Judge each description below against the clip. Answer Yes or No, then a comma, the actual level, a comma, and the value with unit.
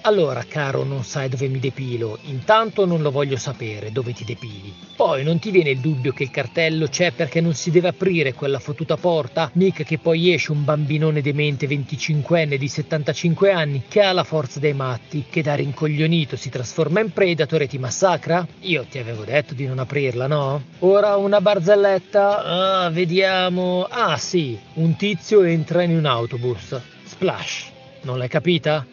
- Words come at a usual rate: No, fast, 175 wpm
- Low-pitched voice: No, medium, 155 Hz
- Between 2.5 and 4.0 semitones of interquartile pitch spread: No, average, 4.6 semitones